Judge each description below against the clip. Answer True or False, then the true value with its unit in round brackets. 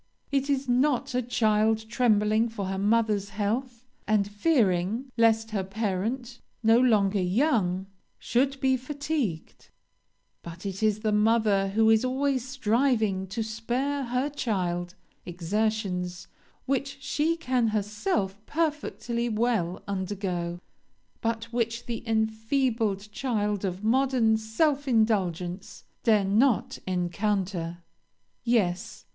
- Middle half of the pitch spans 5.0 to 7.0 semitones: False (4.1 semitones)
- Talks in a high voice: True (220 Hz)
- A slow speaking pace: True (115 wpm)